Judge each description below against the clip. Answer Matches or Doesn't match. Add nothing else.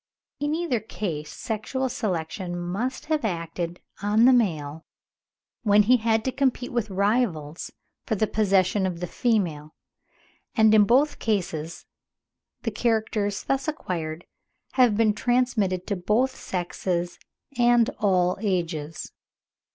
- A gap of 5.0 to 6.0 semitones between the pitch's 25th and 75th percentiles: Matches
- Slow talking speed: Matches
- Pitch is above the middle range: Matches